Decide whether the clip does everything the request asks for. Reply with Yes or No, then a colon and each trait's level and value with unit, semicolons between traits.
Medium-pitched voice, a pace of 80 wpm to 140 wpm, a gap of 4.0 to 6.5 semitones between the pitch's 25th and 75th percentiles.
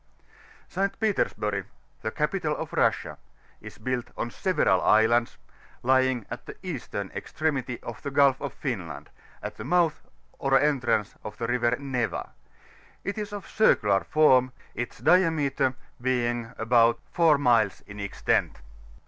No: low, 130 Hz; slow, 135 wpm; average, 4.4 semitones